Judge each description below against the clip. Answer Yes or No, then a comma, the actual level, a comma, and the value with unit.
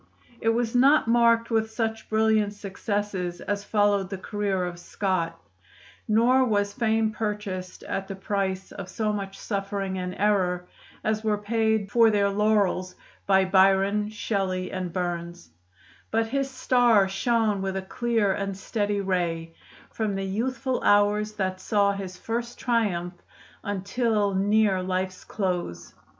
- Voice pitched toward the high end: Yes, high, 205 Hz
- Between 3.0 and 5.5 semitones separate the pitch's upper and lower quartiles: No, narrow, 2.6 semitones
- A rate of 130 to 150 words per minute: Yes, average, 140 wpm